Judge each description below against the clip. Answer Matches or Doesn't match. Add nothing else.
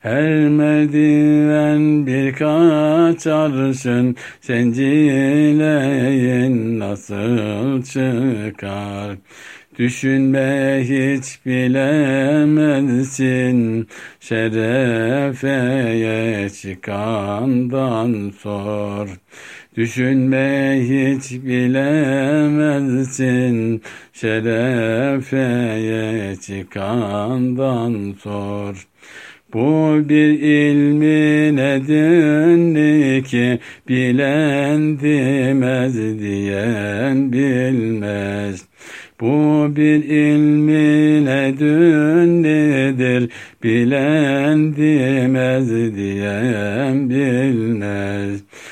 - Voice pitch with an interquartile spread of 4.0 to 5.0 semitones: Matches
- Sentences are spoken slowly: Matches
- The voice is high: Doesn't match